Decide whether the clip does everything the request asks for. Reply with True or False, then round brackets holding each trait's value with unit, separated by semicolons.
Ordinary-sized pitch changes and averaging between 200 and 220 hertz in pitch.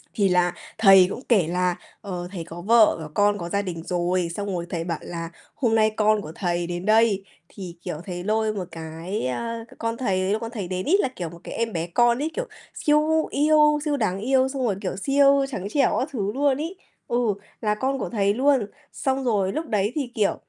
False (6.0 semitones; 210 Hz)